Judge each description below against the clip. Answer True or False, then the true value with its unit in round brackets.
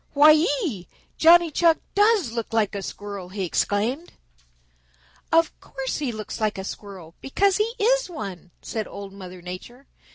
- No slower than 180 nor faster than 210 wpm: False (155 wpm)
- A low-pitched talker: False (230 Hz)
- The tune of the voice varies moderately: False (8.7 semitones)